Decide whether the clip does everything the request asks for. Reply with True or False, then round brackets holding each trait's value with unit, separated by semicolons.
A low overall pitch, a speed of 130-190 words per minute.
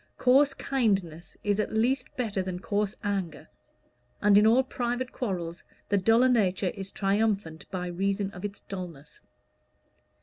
False (200 Hz; 140 wpm)